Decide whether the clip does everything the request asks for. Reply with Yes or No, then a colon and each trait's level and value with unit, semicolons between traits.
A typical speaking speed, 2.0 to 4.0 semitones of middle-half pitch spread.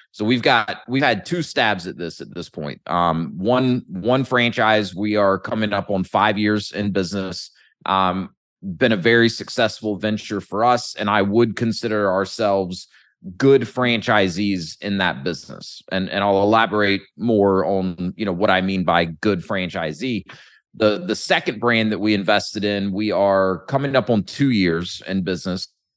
Yes: average, 170 wpm; average, 3.4 semitones